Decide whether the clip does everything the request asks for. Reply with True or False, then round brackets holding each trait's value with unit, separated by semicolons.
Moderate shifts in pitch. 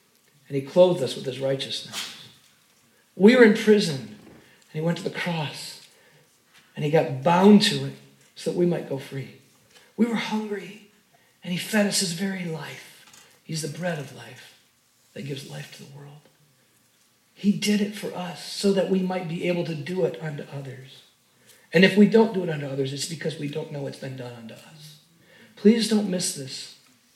False (6.0 semitones)